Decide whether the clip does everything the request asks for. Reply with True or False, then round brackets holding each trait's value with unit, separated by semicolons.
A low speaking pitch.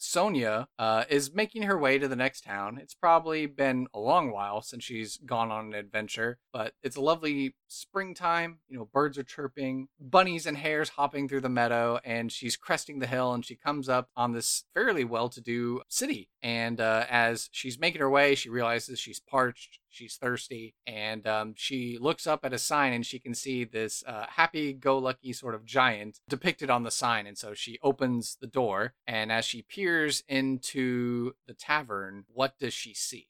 True (125 Hz)